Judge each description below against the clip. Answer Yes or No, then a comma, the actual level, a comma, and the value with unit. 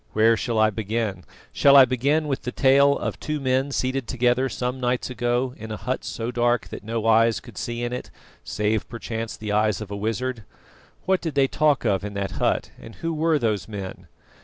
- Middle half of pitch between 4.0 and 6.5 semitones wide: No, average, 3.3 semitones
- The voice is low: Yes, low, 120 Hz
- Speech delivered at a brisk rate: Yes, fast, 210 wpm